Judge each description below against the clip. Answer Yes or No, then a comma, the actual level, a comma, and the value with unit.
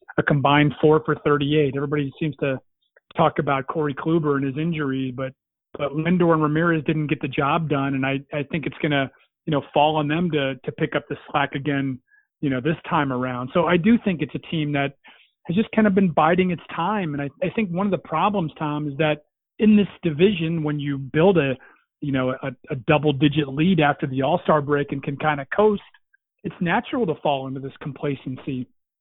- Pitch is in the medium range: Yes, medium, 150 Hz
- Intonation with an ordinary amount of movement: Yes, average, 3.0 semitones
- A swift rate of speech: Yes, fast, 220 wpm